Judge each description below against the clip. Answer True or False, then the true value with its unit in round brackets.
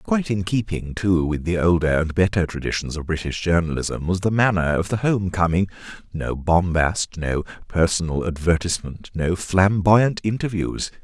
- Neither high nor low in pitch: False (90 Hz)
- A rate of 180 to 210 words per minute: False (150 wpm)